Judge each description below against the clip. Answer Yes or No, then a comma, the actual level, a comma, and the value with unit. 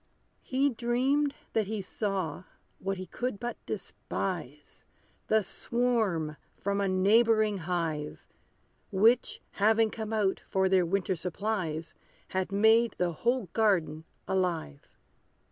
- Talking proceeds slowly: Yes, slow, 115 wpm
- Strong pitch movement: No, average, 3.7 semitones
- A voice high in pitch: Yes, high, 195 Hz